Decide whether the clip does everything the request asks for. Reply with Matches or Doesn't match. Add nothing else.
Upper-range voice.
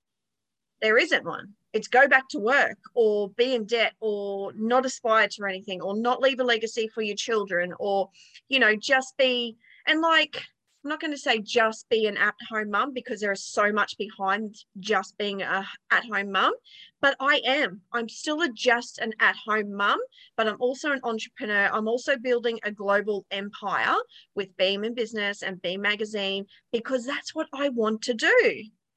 Matches